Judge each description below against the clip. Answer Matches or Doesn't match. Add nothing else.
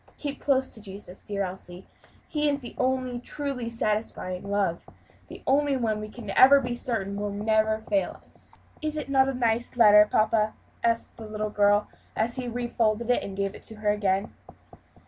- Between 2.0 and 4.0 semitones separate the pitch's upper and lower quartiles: Matches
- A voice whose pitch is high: Matches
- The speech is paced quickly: Doesn't match